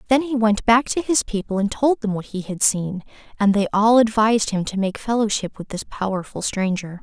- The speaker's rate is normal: No, fast, 220 wpm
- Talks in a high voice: Yes, high, 210 Hz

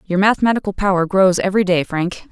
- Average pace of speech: Yes, average, 180 wpm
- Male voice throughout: No, female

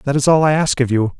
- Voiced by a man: Yes, male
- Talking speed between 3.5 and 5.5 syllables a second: No, 6.1 syllables/s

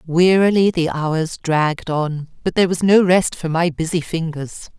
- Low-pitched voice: No, medium, 165 Hz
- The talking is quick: No, average, 175 wpm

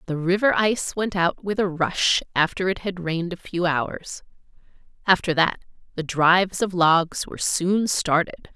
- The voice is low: No, medium, 180 Hz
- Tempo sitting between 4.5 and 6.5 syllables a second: Yes, 4.6 syllables/s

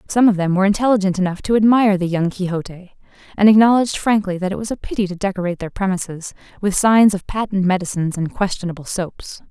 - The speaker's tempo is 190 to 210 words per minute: Yes, average, 195 wpm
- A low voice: No, high, 195 Hz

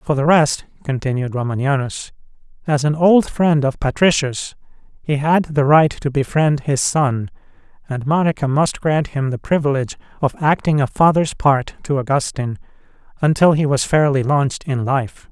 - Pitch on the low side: No, medium, 145 Hz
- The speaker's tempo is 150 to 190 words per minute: Yes, average, 155 wpm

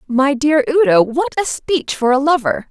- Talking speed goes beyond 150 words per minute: Yes, average, 200 wpm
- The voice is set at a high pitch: Yes, very high, 280 Hz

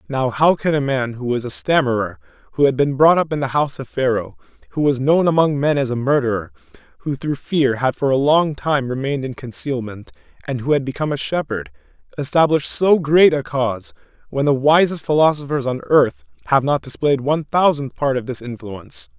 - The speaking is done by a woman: No, male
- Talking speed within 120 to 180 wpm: No, average, 200 wpm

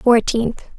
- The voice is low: No, high, 235 Hz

